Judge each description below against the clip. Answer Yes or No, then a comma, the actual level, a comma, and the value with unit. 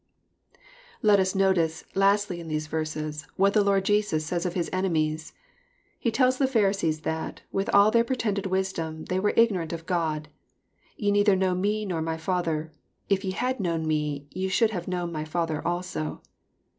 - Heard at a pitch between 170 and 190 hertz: Yes, medium, 185 Hz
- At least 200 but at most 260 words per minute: No, average, 180 wpm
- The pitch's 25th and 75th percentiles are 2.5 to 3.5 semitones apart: No, average, 3.9 semitones